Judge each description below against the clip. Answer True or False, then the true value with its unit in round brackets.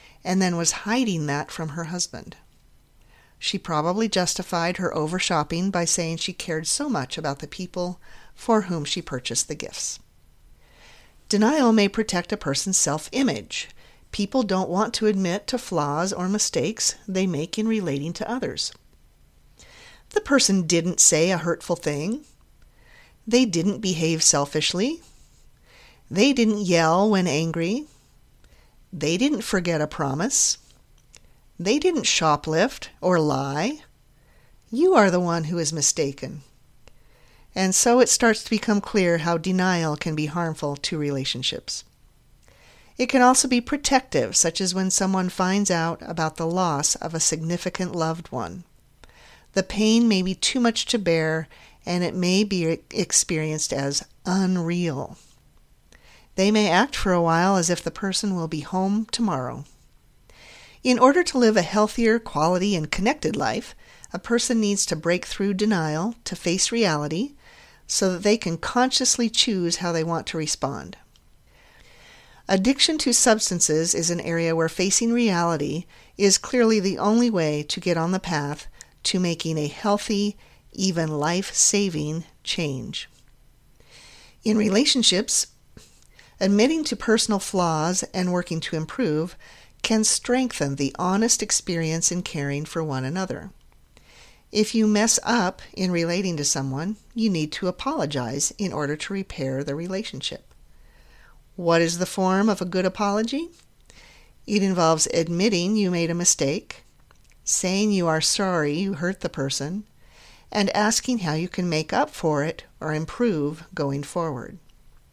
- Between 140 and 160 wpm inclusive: True (145 wpm)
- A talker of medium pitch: True (180 Hz)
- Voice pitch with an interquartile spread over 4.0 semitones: True (4.7 semitones)